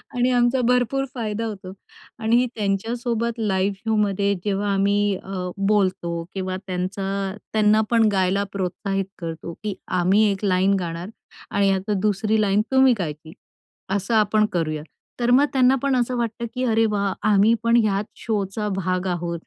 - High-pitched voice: Yes, high, 200 Hz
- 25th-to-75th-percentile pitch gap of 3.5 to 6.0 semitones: No, average, 2.9 semitones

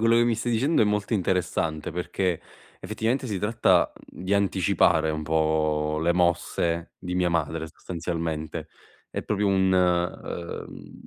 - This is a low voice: Yes, very low, 90 Hz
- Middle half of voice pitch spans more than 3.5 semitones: Yes, average, 4.0 semitones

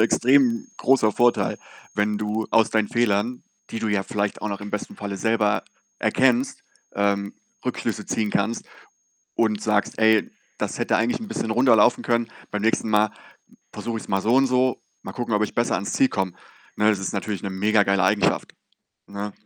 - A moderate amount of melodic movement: No, narrow, 2.3 semitones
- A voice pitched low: Yes, low, 110 Hz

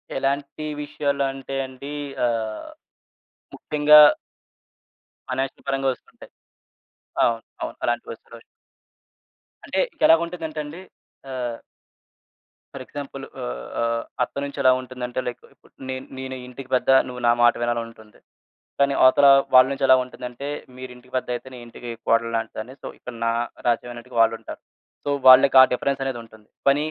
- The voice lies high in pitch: No, low, 130 Hz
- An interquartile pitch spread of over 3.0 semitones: No, narrow, 2.5 semitones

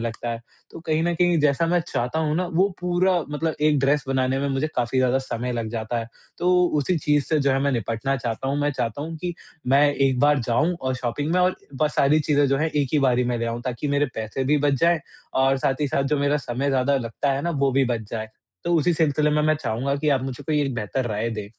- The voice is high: No, medium, 140 Hz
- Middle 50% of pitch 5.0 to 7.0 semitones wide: No, average, 3.5 semitones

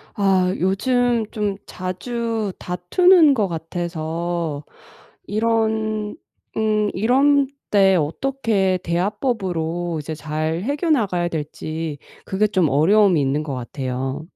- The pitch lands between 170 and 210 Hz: Yes, high, 190 Hz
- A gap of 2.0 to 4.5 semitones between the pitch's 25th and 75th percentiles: No, average, 5.3 semitones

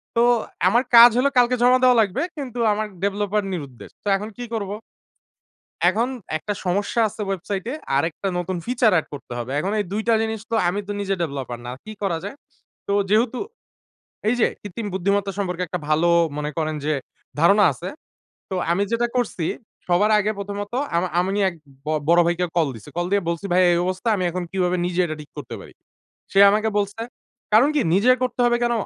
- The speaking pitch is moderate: No, high, 200 Hz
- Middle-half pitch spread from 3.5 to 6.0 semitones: Yes, average, 4.0 semitones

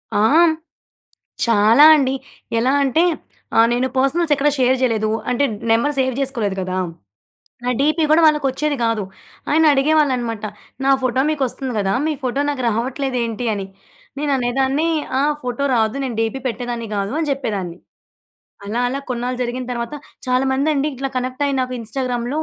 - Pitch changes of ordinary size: Yes, average, 3.0 semitones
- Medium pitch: No, very high, 255 Hz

